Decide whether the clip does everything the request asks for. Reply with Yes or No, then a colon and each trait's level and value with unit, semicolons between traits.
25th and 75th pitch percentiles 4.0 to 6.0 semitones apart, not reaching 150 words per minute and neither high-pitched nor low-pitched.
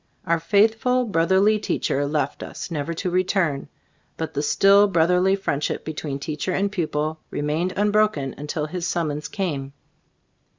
Yes: average, 4.7 semitones; average, 140 wpm; medium, 170 Hz